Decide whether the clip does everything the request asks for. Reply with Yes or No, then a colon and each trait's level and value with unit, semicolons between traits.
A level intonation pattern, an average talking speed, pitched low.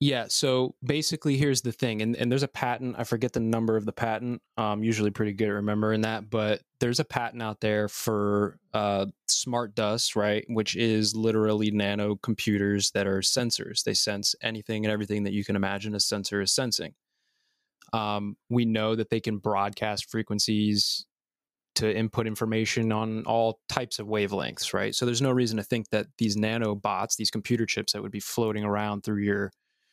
Yes: narrow, 2.0 semitones; average, 190 wpm; low, 110 Hz